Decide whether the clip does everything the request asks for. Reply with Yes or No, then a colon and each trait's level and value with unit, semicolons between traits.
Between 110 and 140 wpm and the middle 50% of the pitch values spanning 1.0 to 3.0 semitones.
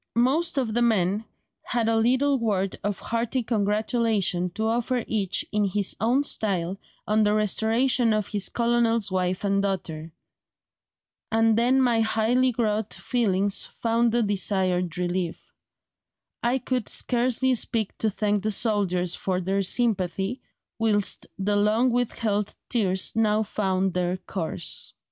No: slow, 135 wpm; average, 3.4 semitones